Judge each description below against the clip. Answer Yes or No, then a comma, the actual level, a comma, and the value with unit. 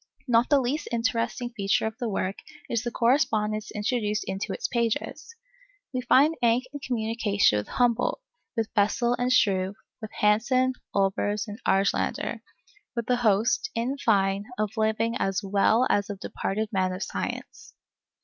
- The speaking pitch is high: Yes, high, 220 Hz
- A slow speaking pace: No, average, 150 wpm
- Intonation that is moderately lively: Yes, average, 3.2 semitones